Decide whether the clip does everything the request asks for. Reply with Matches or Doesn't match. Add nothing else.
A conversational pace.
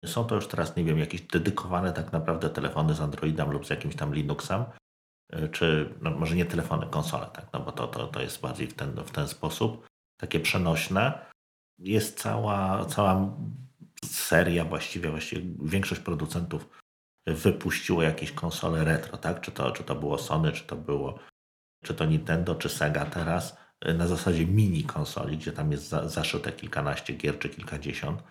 Doesn't match